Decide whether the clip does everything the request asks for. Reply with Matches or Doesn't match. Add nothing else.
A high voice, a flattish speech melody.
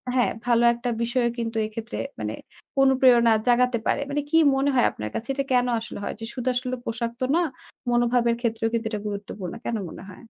Matches